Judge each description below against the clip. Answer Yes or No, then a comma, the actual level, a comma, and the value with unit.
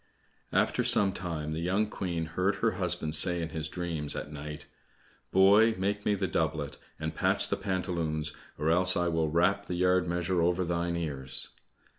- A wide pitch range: No, average, 2.9 semitones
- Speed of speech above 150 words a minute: Yes, average, 175 wpm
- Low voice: Yes, very low, 85 Hz